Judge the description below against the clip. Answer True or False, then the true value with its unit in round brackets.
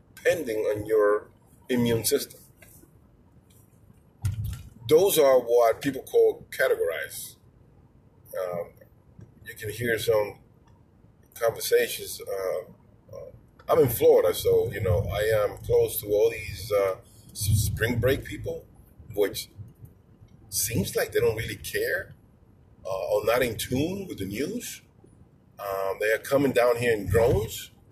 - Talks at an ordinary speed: False (125 wpm)